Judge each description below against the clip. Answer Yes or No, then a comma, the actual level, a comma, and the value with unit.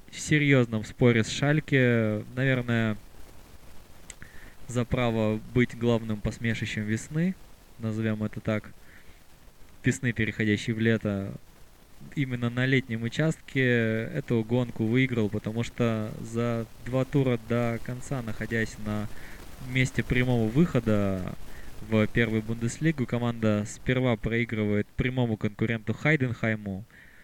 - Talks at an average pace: No, slow, 105 wpm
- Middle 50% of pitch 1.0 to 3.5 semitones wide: Yes, narrow, 2.5 semitones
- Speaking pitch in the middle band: No, low, 115 Hz